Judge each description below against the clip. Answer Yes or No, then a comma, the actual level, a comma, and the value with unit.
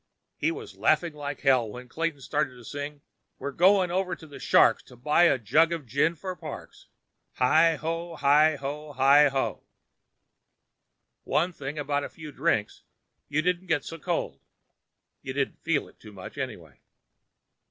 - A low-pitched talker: No, medium, 150 Hz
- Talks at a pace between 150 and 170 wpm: Yes, average, 165 wpm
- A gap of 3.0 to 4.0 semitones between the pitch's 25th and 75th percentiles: Yes, average, 3.5 semitones